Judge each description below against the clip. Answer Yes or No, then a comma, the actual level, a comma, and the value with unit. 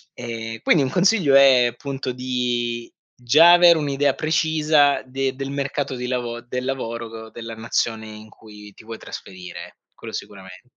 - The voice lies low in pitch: Yes, low, 125 Hz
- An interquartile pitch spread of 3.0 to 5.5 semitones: Yes, average, 3.6 semitones